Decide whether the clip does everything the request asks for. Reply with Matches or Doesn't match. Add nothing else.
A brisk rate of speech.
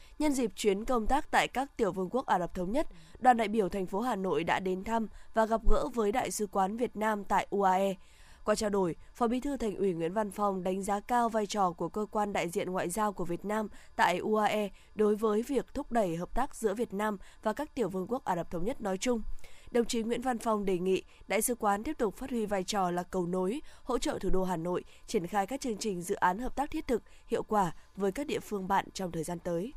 Matches